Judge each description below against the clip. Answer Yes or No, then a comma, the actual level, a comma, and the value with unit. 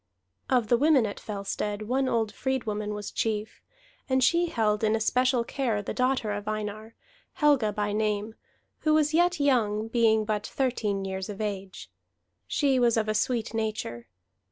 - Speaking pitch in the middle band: No, high, 220 Hz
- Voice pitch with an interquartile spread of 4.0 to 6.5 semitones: No, average, 3.5 semitones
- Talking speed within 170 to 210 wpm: No, average, 160 wpm